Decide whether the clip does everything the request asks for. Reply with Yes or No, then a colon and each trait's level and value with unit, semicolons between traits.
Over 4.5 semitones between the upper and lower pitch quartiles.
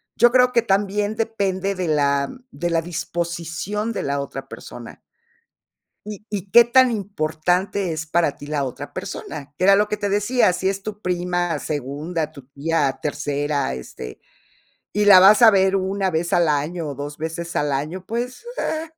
Yes: wide, 5.4 semitones